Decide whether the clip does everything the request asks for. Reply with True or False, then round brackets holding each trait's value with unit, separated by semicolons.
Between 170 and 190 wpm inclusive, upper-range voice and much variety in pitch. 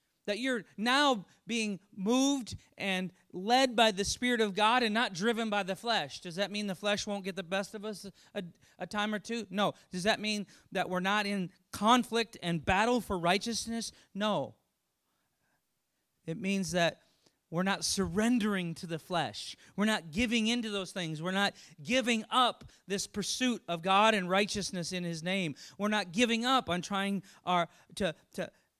False (175 wpm; 200 Hz; 3.5 semitones)